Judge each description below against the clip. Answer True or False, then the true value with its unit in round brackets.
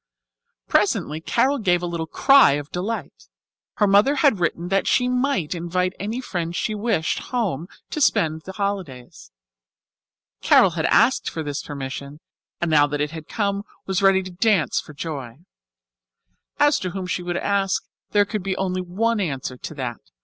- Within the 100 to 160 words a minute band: False (175 wpm)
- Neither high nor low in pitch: True (180 Hz)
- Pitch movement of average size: True (4.6 semitones)